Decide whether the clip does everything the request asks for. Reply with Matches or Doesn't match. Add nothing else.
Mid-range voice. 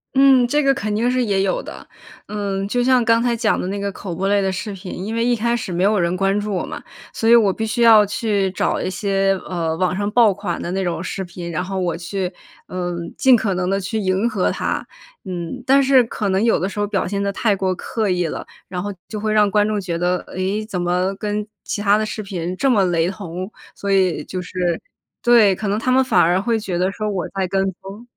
Doesn't match